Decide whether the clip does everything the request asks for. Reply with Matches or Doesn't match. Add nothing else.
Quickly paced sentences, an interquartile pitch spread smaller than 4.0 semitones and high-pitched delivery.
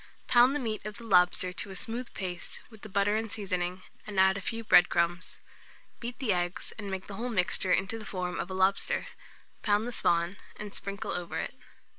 Matches